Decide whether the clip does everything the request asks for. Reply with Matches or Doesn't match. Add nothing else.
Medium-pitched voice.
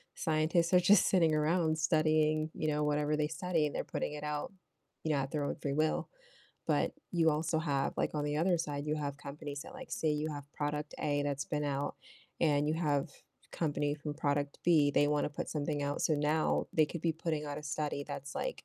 Matches